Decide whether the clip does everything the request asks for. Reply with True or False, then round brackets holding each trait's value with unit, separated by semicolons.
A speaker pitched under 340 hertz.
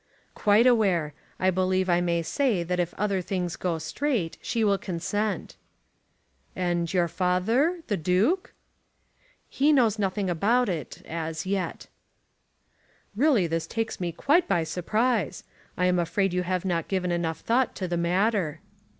True (185 Hz)